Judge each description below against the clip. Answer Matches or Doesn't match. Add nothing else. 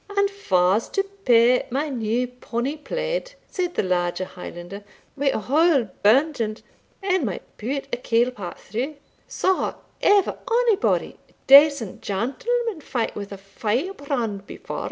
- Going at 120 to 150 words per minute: Matches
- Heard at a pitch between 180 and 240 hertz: Doesn't match